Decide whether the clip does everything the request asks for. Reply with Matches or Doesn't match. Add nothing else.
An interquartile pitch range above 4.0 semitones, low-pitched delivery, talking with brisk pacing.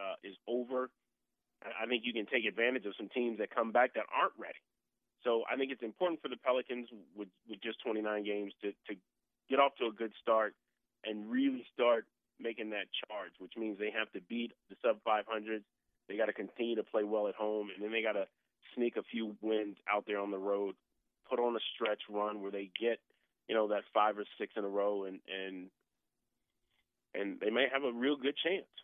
Doesn't match